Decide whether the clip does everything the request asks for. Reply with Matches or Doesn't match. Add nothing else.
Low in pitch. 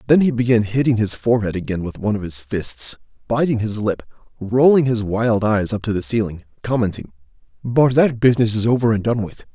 Matches